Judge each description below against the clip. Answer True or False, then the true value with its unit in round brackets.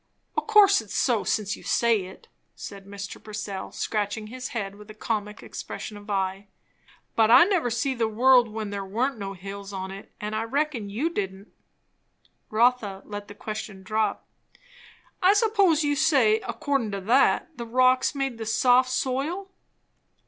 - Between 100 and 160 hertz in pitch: False (220 Hz)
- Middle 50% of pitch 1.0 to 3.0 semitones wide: False (4.3 semitones)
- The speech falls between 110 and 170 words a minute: True (165 wpm)